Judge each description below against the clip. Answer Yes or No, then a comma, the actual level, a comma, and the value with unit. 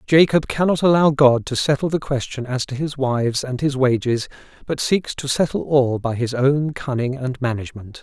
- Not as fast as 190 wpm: No, average, 195 wpm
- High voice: No, low, 135 Hz